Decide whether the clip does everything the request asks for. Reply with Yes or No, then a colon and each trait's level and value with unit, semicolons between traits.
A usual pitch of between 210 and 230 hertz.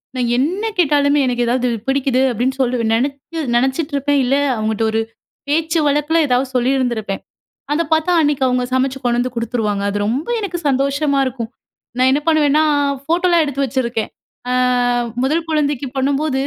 No: very high, 270 Hz